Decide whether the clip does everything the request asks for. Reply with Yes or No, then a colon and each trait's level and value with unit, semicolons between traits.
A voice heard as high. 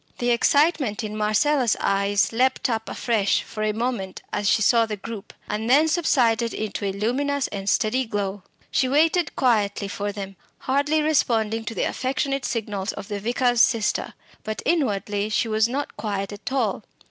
Yes: high, 225 Hz